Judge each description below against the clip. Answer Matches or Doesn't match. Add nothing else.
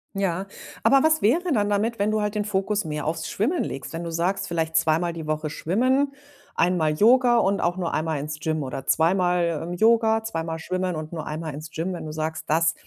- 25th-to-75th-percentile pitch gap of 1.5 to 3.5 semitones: Doesn't match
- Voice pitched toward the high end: Doesn't match